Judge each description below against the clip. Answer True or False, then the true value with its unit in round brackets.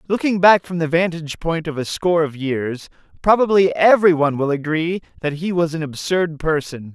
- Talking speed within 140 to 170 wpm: False (190 wpm)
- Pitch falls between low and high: True (165 Hz)